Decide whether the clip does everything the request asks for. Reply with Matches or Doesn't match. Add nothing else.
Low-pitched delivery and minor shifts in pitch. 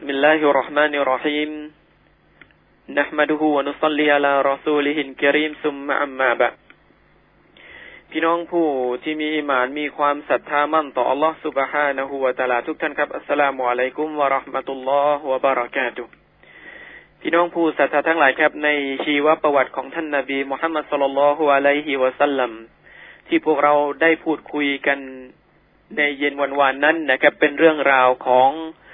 Doesn't match